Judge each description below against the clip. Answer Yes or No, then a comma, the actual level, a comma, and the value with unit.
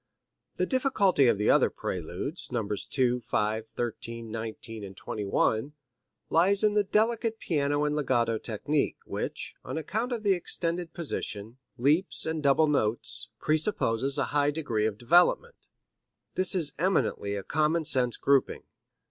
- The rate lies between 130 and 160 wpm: Yes, average, 140 wpm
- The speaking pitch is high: No, medium, 140 Hz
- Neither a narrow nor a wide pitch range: No, wide, 7.2 semitones